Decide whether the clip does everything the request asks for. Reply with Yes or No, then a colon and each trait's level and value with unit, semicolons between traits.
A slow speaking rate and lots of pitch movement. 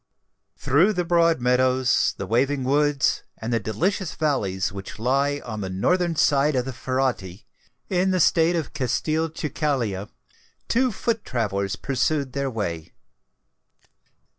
Yes: slow, 130 wpm; wide, 5.8 semitones